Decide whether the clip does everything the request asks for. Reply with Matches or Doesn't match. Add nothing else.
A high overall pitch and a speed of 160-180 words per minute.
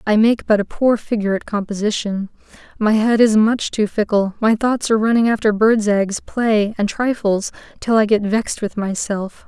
Doesn't match